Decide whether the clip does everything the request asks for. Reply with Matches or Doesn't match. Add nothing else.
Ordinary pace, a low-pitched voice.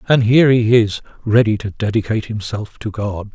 Matches